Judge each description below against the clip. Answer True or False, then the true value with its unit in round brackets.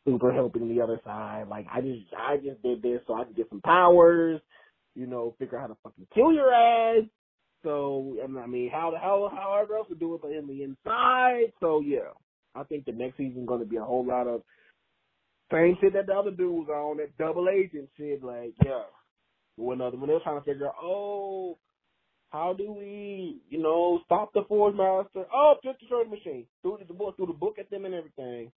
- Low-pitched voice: False (160 Hz)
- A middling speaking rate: False (220 wpm)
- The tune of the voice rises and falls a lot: True (7.7 semitones)